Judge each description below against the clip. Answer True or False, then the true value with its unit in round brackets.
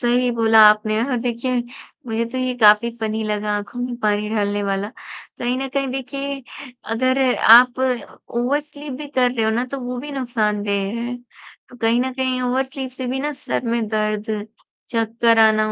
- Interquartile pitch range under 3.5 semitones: True (3.1 semitones)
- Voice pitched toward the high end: True (240 Hz)